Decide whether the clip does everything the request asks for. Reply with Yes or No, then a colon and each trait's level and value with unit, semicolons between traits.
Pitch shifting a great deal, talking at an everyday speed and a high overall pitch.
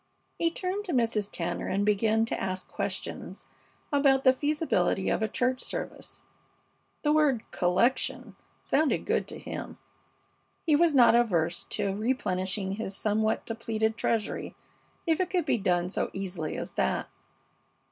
Yes: wide, 5.7 semitones; average, 145 wpm; high, 225 Hz